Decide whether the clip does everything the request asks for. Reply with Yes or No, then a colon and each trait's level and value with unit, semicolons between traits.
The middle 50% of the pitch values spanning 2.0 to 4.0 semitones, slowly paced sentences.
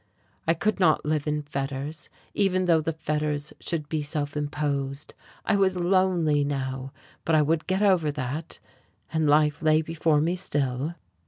No: narrow, 2.4 semitones; average, 160 wpm